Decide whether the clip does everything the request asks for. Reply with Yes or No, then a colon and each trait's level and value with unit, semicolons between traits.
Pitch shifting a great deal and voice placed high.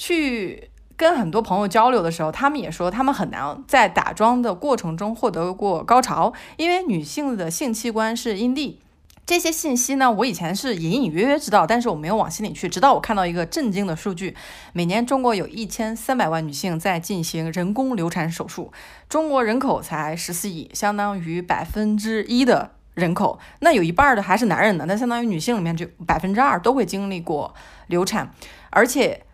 Yes: wide, 5.7 semitones; high, 215 Hz